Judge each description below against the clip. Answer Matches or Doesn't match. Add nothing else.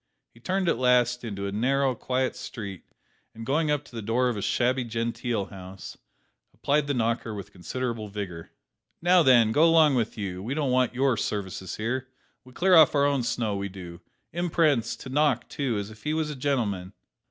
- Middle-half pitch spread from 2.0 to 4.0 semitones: Doesn't match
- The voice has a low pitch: Matches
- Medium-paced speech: Matches